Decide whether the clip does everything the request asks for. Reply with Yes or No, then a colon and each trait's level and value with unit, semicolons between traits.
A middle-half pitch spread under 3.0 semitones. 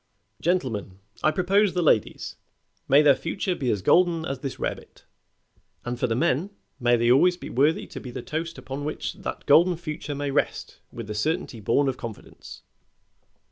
No: wide, 5.6 semitones